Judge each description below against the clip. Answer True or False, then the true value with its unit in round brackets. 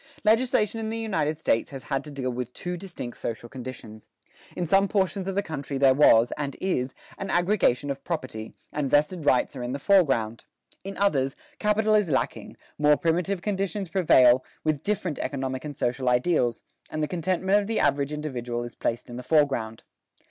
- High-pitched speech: False (150 Hz)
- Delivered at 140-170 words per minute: False (185 wpm)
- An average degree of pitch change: False (6.7 semitones)